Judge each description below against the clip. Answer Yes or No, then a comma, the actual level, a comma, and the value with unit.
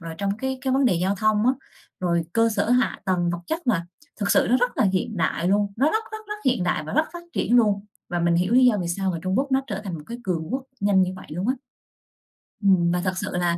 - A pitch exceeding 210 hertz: No, high, 200 Hz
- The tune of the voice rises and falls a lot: Yes, wide, 5.8 semitones